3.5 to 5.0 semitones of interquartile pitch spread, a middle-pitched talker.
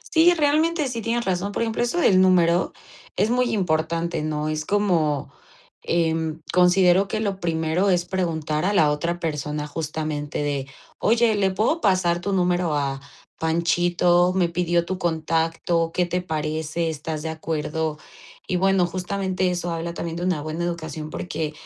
No: average, 3.0 semitones; medium, 170 Hz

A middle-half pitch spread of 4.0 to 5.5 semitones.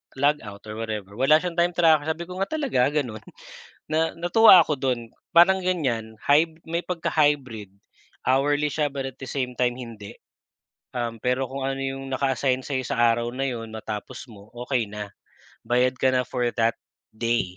Yes: average, 4.7 semitones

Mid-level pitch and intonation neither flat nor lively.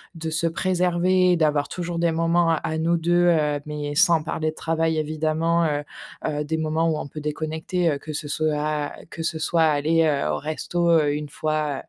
No: medium, 160 Hz; narrow, 1.8 semitones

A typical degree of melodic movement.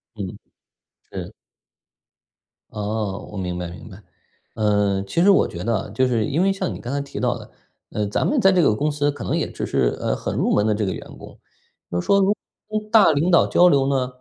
No: wide, 9.0 semitones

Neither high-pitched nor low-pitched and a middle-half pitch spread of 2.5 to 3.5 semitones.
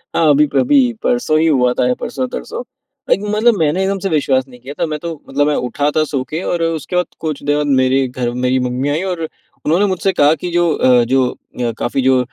No: medium, 150 Hz; average, 4.7 semitones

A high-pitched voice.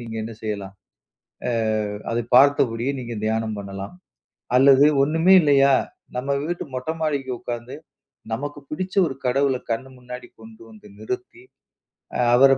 No: low, 125 Hz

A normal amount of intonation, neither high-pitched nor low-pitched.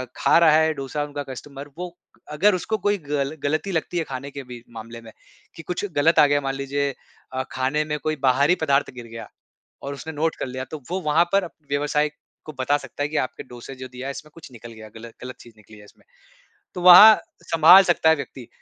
Yes: average, 3.6 semitones; medium, 145 Hz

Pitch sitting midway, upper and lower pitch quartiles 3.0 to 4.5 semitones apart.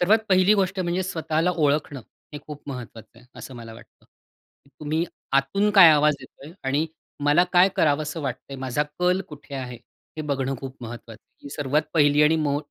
Yes: medium, 150 Hz; average, 3.4 semitones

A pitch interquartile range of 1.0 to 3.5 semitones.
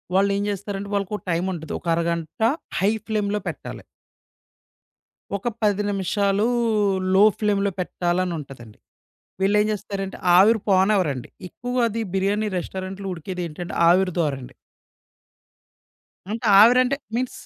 Yes: average, 2.9 semitones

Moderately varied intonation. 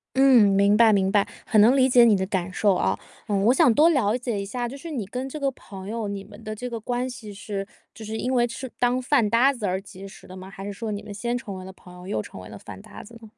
Yes: average, 4.0 semitones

